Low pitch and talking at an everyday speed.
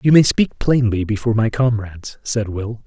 Yes: low, 115 Hz; average, 190 wpm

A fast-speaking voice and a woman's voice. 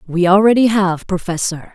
No: average, 140 wpm; female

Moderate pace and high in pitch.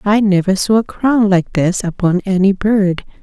Yes: average, 185 wpm; high, 195 Hz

